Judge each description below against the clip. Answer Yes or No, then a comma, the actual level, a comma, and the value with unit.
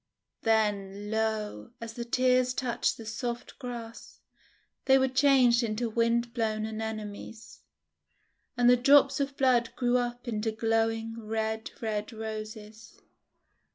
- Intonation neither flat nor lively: No, narrow, 1.9 semitones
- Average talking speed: No, slow, 120 wpm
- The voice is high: Yes, high, 225 Hz